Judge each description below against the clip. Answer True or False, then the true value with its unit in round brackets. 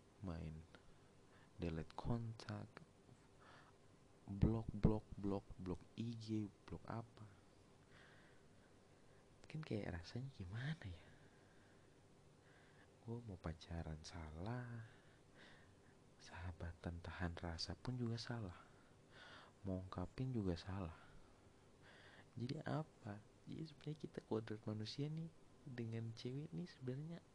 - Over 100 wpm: False (90 wpm)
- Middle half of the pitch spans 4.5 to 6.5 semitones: True (5.5 semitones)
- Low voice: True (105 Hz)